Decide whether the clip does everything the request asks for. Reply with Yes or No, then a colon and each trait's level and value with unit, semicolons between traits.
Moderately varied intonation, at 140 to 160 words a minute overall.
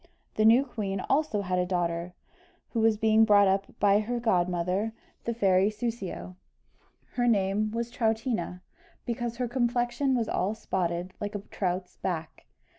Yes: average, 4.2 semitones; average, 150 wpm